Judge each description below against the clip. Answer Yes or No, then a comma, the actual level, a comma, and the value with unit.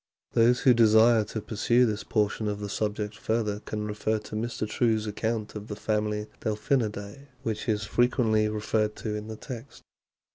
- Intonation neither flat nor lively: No, narrow, 1.3 semitones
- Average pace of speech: Yes, average, 170 wpm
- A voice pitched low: Yes, low, 110 Hz